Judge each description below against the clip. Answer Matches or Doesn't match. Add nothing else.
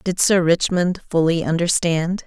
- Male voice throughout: Doesn't match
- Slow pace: Matches